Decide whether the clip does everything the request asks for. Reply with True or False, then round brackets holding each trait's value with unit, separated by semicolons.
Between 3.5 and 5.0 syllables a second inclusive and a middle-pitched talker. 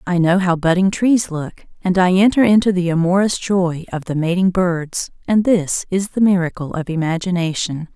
True (4.9 syllables/s; 180 Hz)